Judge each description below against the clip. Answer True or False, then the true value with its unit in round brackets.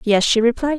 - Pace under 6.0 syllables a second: True (5.8 syllables/s)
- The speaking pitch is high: True (240 Hz)